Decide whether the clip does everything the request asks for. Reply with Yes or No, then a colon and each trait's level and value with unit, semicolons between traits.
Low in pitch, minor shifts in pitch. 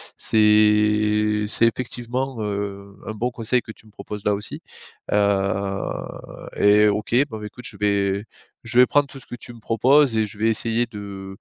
Yes: low, 105 Hz; narrow, 2.3 semitones